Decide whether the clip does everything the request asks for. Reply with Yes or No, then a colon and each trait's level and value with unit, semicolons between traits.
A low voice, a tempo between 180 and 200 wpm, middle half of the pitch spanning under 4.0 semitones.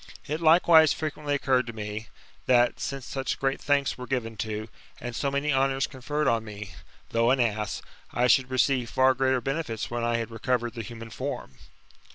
Yes: low, 125 Hz; average, 185 wpm; average, 3.1 semitones